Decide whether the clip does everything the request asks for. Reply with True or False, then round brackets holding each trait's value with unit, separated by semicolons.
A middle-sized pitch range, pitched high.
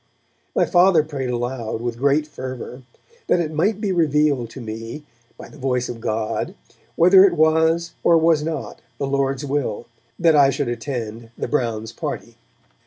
False (4.9 semitones; 140 Hz)